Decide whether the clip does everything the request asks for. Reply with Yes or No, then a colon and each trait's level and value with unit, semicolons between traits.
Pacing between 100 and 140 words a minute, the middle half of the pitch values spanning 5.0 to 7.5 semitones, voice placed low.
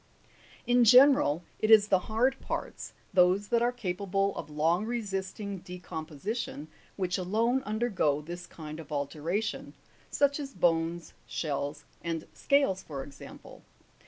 No: slow, 135 wpm; wide, 5.5 semitones; high, 190 Hz